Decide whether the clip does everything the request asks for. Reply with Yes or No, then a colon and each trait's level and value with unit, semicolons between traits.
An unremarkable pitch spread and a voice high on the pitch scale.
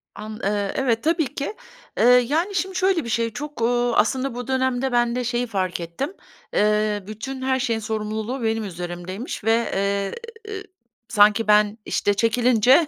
Yes: average, 3.9 semitones; high, 235 Hz